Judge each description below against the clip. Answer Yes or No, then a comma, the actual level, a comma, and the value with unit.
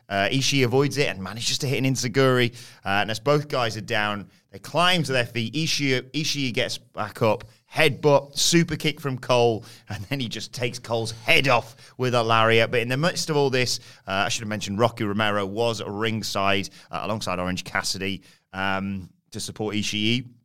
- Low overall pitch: Yes, low, 120 Hz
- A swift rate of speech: No, average, 195 wpm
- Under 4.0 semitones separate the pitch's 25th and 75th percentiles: No, average, 4.3 semitones